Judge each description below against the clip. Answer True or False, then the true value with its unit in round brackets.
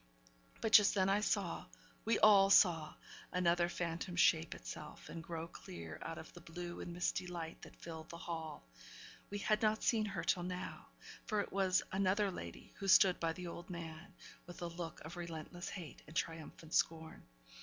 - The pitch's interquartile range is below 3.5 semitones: True (2.9 semitones)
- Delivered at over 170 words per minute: True (180 wpm)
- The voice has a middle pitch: True (175 Hz)